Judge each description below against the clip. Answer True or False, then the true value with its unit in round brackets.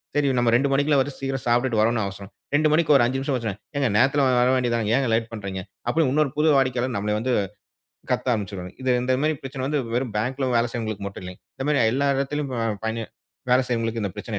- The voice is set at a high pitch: False (125 Hz)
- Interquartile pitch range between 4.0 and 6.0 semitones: False (3.5 semitones)